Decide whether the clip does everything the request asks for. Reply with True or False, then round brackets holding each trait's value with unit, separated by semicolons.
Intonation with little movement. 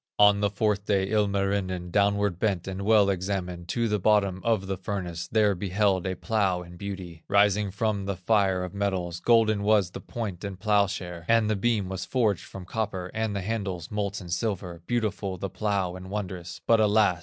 True (2.3 semitones)